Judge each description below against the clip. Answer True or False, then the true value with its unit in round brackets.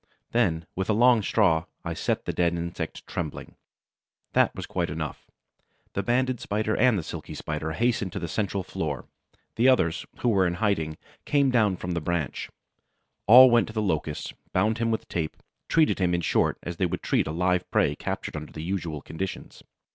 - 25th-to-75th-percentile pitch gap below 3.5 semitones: False (5.3 semitones)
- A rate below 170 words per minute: False (190 wpm)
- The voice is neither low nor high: False (95 Hz)